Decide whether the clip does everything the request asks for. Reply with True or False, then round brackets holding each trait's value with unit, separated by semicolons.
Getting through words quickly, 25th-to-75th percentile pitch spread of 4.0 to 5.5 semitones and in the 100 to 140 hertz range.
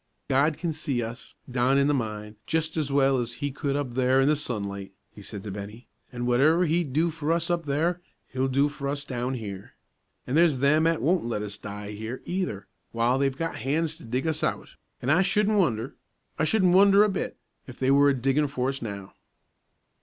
True (215 wpm; 4.9 semitones; 135 Hz)